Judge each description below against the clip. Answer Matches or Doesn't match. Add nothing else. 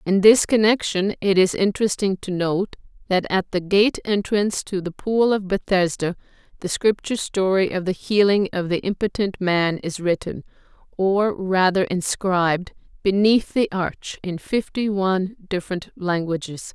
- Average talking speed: Matches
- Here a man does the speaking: Doesn't match